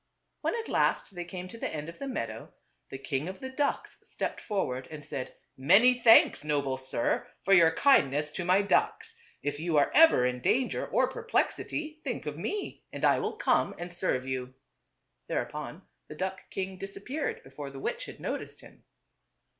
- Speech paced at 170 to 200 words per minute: Yes, average, 190 wpm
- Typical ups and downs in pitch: No, wide, 8.8 semitones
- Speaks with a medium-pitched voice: Yes, medium, 175 Hz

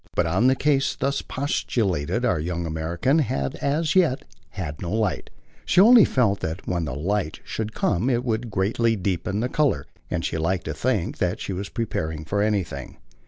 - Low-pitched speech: Yes, low, 100 Hz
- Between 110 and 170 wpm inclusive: No, average, 180 wpm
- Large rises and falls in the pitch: Yes, wide, 7.1 semitones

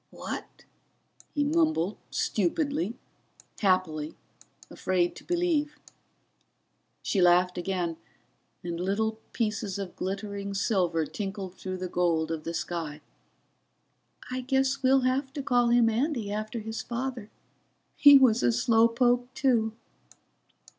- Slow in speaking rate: Yes, slow, 120 wpm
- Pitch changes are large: Yes, wide, 5.9 semitones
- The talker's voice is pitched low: No, high, 215 Hz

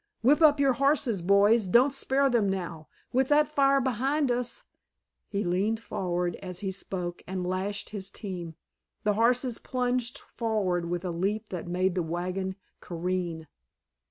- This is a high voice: Yes, high, 200 Hz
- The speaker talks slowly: No, average, 155 wpm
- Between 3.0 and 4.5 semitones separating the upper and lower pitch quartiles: No, wide, 5.6 semitones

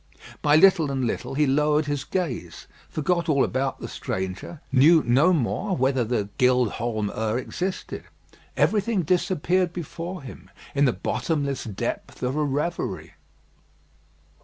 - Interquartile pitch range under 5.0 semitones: No, average, 5.3 semitones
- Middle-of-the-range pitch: Yes, medium, 145 Hz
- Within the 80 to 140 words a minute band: Yes, slow, 135 wpm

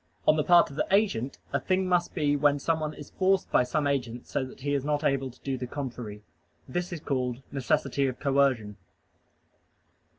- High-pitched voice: No, medium, 140 Hz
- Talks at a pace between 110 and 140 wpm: No, average, 195 wpm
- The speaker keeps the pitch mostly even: No, average, 3.2 semitones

